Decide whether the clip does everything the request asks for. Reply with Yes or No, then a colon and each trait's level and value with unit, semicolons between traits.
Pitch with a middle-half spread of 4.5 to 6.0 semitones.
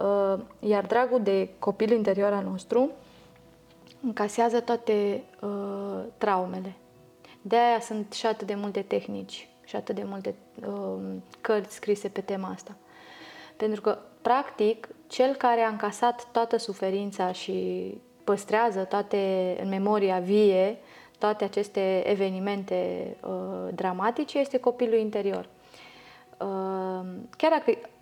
No: average, 3.2 semitones